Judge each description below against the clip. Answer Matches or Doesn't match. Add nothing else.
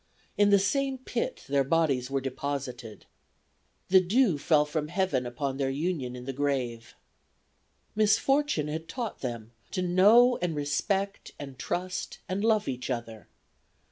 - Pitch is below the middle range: Doesn't match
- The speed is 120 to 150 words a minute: Matches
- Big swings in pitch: Matches